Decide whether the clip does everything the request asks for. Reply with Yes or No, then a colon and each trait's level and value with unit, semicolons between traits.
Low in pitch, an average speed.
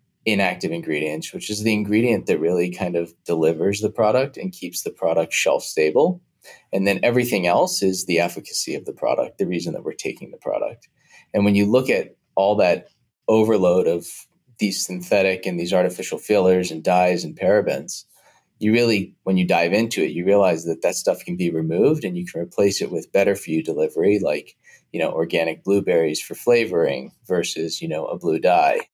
Yes: low, 105 Hz; average, 195 wpm